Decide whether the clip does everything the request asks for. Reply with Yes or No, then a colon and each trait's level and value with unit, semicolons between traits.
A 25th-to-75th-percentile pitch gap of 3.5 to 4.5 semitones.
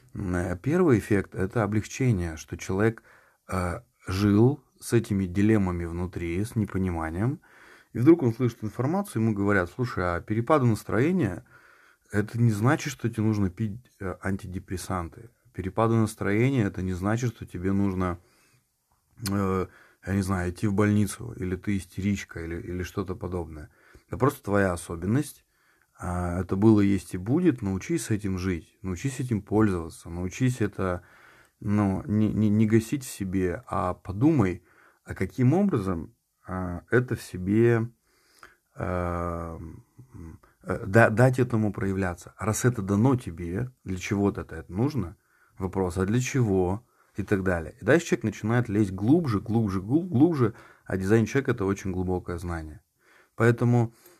Yes: average, 4.1 semitones